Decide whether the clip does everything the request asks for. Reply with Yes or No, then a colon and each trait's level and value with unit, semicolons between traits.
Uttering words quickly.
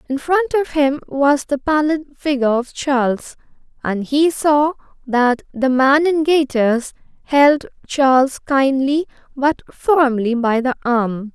No: slow, 135 wpm